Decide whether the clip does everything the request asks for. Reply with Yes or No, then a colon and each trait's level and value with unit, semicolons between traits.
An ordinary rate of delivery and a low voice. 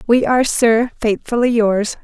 No: average, 145 wpm; high, 230 Hz